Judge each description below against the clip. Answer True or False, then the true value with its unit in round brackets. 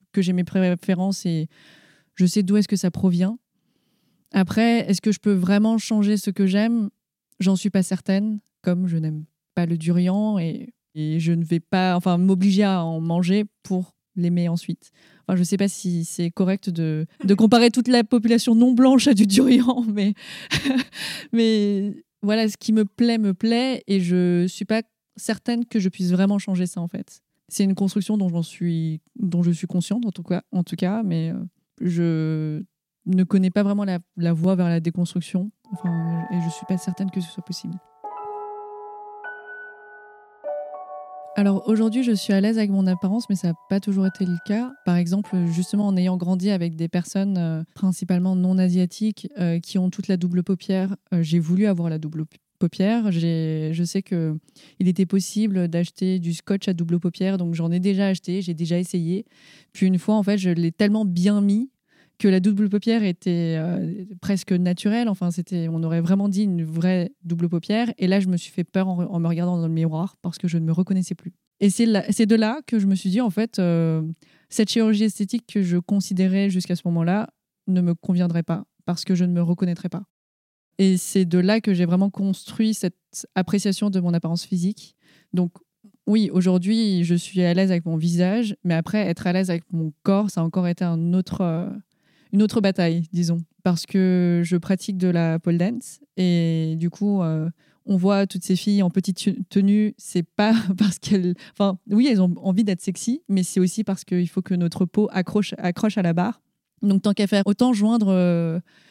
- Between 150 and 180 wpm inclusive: False (200 wpm)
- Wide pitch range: False (2.9 semitones)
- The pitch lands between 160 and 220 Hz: True (190 Hz)